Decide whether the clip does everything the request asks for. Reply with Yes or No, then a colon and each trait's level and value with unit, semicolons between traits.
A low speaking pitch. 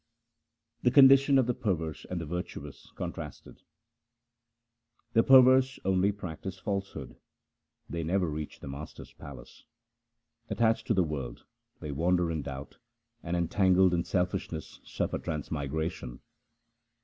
Yes: very low, 90 Hz